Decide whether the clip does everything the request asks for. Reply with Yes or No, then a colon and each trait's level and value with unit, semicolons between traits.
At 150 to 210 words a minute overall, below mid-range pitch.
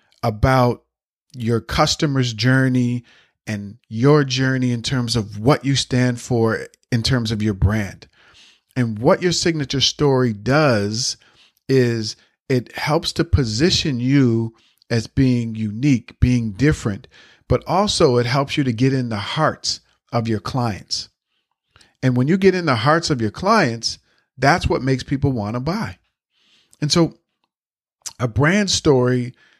No: average, 140 wpm; low, 125 Hz